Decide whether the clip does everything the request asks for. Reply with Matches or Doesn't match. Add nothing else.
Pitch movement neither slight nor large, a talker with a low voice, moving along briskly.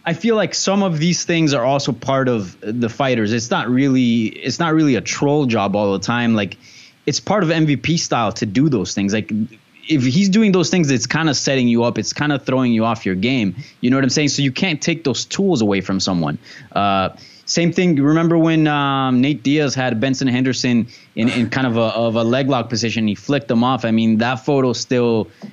Matches